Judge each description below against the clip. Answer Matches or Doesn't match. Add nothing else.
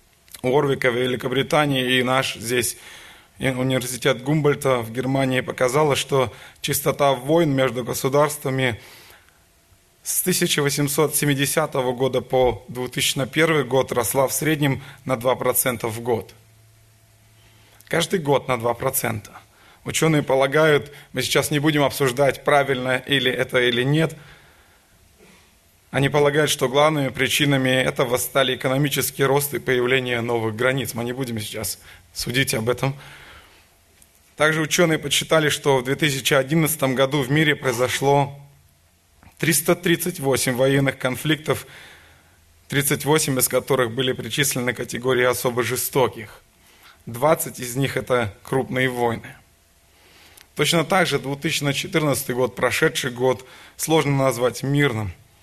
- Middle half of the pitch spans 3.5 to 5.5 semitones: Doesn't match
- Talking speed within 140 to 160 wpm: Doesn't match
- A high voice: Doesn't match